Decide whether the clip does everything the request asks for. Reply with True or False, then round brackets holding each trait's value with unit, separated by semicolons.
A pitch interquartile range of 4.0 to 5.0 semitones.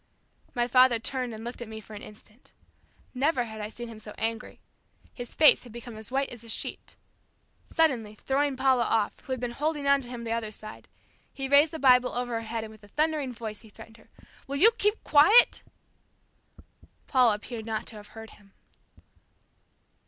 False (3.4 semitones)